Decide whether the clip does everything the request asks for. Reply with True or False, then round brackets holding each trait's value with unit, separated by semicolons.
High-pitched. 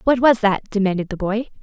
True (215 Hz)